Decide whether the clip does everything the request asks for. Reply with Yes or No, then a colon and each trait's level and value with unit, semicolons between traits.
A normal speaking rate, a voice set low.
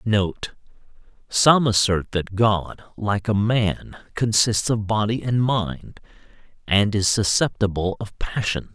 No: slow, 115 wpm; low, 105 Hz